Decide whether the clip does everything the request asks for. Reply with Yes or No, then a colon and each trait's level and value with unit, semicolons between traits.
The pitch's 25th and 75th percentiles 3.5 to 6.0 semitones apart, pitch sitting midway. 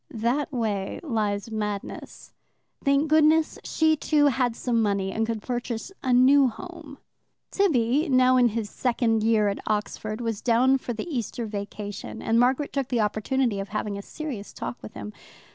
No: average, 4.1 semitones; high, 235 Hz